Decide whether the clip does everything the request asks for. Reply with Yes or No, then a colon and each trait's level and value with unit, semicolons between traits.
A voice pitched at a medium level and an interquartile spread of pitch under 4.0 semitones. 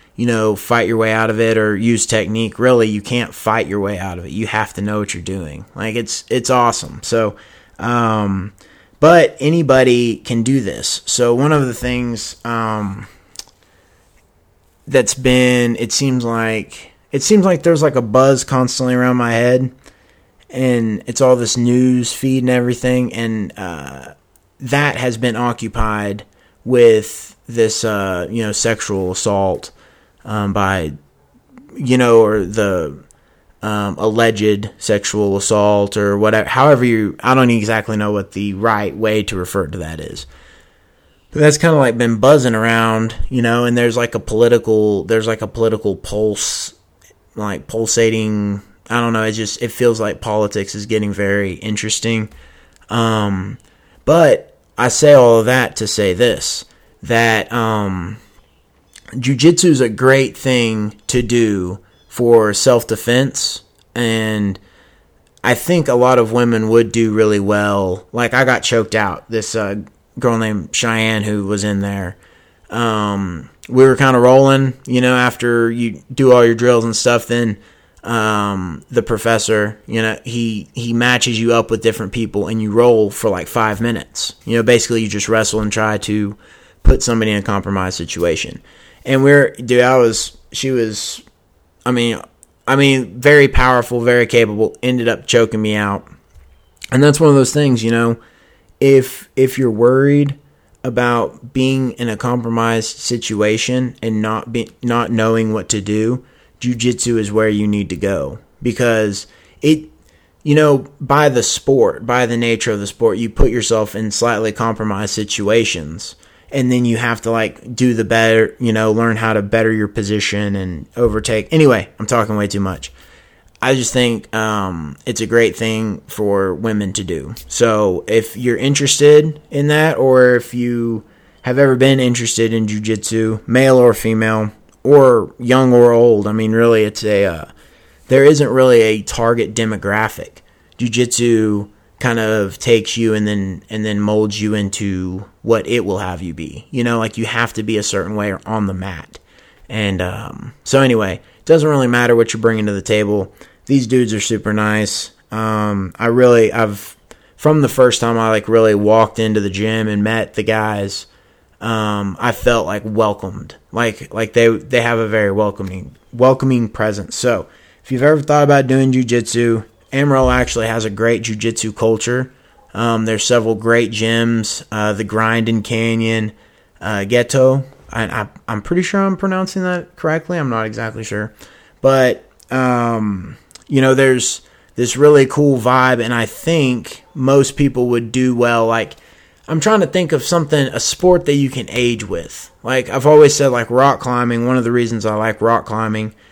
No: low, 115 Hz; average, 2.8 semitones